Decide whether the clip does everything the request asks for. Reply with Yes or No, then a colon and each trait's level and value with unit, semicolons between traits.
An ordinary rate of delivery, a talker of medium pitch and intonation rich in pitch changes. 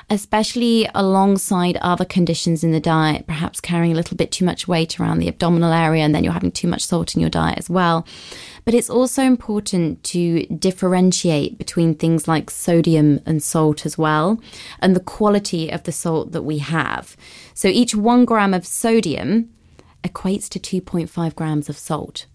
No: average, 175 wpm; medium, 170 Hz; average, 3.5 semitones